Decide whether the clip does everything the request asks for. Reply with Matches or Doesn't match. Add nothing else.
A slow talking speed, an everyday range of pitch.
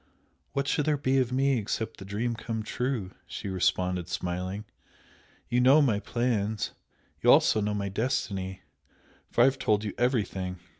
Doesn't match